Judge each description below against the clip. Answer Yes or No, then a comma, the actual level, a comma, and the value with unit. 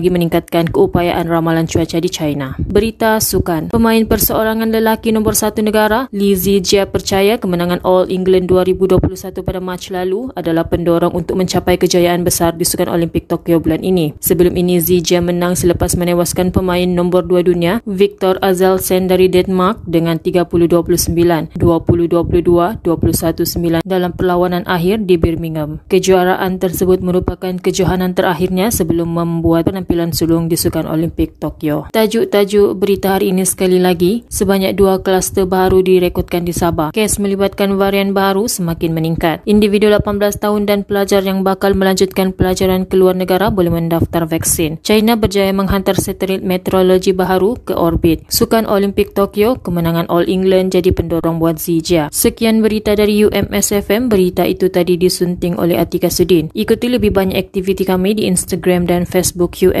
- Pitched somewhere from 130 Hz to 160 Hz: No, medium, 185 Hz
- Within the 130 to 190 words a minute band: Yes, average, 145 wpm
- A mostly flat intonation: Yes, narrow, 2.2 semitones